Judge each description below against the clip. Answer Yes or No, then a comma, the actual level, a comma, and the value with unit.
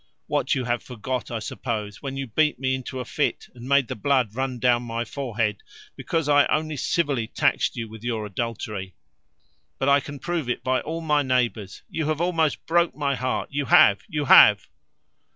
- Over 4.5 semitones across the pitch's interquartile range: No, average, 3.8 semitones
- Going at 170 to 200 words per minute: Yes, average, 190 wpm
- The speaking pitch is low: Yes, low, 130 Hz